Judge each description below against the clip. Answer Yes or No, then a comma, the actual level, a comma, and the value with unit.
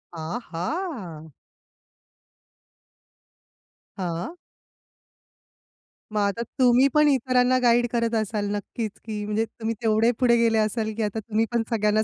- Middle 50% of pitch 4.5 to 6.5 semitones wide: No, narrow, 2.5 semitones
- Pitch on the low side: No, high, 225 Hz